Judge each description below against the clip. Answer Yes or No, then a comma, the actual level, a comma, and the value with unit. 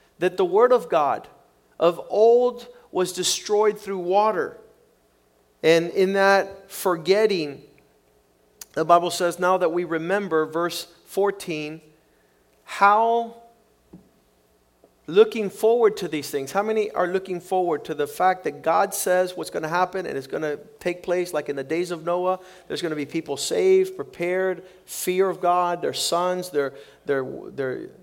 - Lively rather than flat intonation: No, average, 3.9 semitones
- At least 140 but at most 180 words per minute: Yes, average, 155 wpm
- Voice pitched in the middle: Yes, medium, 180 Hz